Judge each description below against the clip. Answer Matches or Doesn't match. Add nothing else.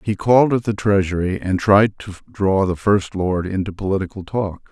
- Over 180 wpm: Matches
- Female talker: Doesn't match